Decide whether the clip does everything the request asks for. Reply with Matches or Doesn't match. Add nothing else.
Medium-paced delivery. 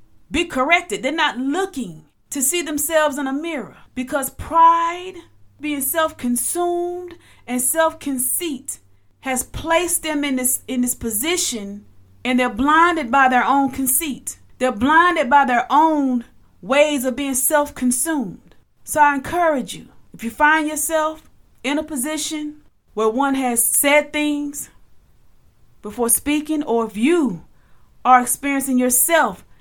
Doesn't match